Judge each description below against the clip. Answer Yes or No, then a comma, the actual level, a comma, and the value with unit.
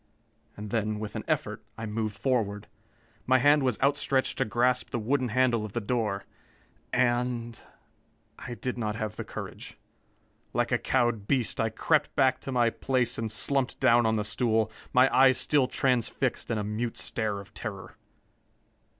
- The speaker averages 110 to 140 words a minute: No, average, 165 wpm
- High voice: No, low, 120 Hz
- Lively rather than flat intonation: No, average, 3.0 semitones